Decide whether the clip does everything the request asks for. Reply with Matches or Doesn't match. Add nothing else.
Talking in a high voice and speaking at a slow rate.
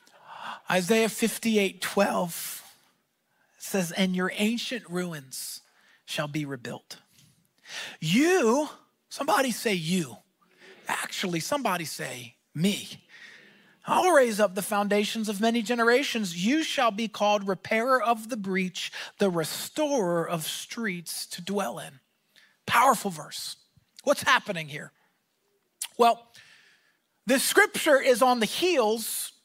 Matches